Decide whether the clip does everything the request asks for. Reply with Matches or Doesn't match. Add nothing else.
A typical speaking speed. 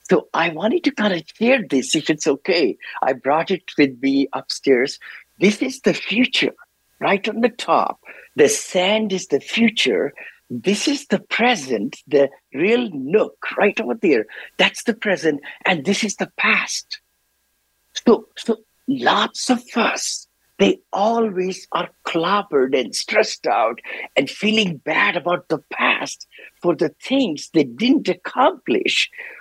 Matches